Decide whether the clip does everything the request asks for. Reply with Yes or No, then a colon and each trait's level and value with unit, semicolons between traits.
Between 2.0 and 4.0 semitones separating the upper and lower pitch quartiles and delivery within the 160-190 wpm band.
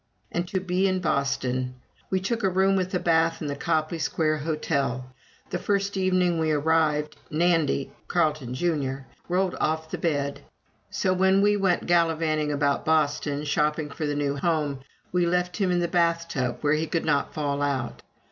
Yes: average, 3.6 semitones; average, 175 wpm